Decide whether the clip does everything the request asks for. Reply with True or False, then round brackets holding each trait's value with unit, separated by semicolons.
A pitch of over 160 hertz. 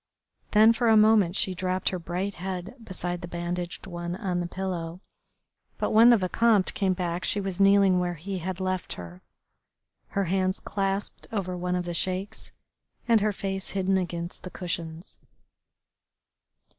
True (185 Hz)